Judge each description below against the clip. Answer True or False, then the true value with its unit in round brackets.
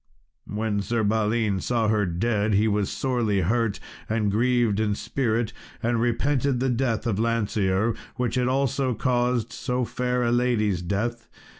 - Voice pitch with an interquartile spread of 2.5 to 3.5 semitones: True (2.8 semitones)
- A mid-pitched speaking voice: False (115 Hz)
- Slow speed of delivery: False (150 wpm)